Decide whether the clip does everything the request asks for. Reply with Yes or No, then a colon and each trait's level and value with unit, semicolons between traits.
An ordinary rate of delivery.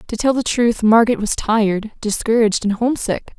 Yes: average, 175 wpm